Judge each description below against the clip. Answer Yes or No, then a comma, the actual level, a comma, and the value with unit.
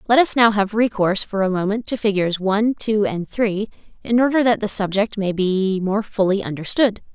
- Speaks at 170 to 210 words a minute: Yes, average, 200 wpm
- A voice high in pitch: Yes, high, 205 Hz